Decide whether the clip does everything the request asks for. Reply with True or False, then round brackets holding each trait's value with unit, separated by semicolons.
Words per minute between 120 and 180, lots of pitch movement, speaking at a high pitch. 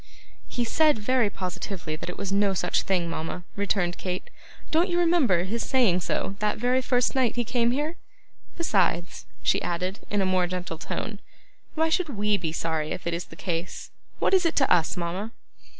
False (190 wpm; 6.0 semitones; 200 Hz)